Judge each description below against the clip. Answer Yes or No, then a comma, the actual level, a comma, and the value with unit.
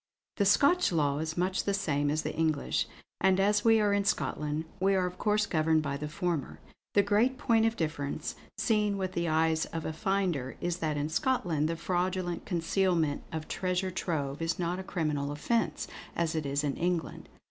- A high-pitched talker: No, medium, 170 Hz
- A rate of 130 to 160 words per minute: No, average, 190 wpm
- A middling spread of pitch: Yes, average, 4.0 semitones